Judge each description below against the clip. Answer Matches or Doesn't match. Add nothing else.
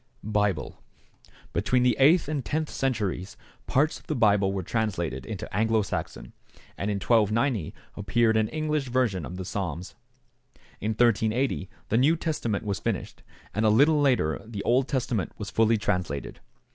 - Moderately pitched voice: Doesn't match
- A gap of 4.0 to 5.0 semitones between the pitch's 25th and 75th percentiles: Matches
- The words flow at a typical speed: Matches